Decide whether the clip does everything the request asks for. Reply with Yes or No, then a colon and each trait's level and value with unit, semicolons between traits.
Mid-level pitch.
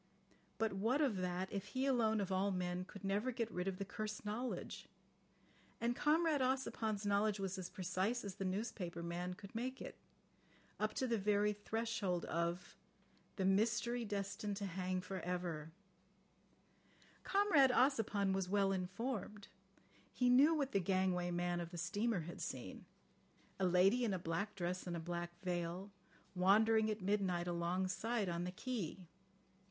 No: high, 195 Hz